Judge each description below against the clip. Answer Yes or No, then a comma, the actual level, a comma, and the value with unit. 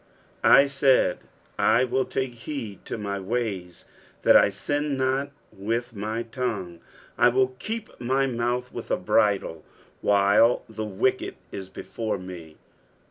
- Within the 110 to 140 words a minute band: Yes, slow, 135 wpm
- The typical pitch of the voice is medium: No, low, 115 Hz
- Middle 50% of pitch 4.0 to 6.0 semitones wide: Yes, average, 4.6 semitones